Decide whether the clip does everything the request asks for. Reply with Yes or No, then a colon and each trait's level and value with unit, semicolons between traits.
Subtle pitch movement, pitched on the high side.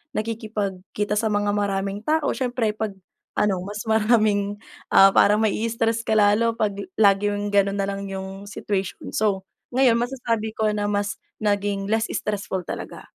Yes: narrow, 1.8 semitones; high, 205 Hz